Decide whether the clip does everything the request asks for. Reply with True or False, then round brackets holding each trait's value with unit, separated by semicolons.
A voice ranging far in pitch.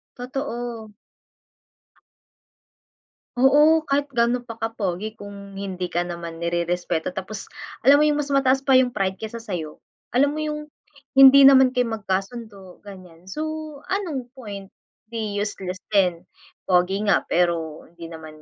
True (6.2 semitones)